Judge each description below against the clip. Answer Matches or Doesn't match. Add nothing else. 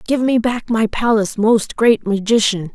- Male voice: Doesn't match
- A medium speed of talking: Matches